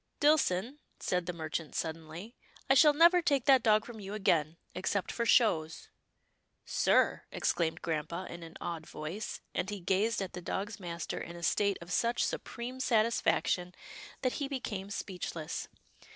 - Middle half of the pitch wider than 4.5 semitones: Yes, wide, 5.6 semitones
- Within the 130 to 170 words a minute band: Yes, average, 165 wpm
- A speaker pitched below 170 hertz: No, high, 195 Hz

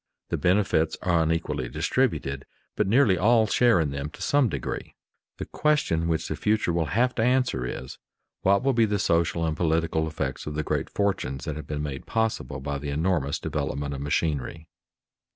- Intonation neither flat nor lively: No, wide, 6.2 semitones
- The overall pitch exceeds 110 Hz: No, very low, 80 Hz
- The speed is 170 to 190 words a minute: Yes, average, 185 wpm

